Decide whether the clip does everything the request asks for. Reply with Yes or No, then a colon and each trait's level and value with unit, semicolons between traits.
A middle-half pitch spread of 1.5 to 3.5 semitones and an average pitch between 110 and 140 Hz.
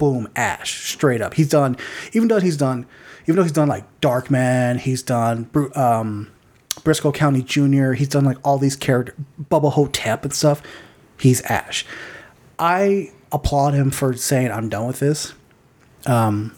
Yes: average, 3.0 semitones; low, 135 Hz